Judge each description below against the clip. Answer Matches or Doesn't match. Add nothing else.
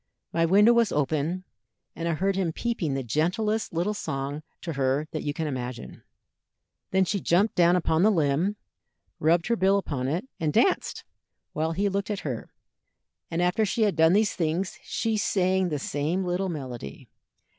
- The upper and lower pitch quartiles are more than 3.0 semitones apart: Matches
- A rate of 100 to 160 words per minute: Doesn't match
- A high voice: Doesn't match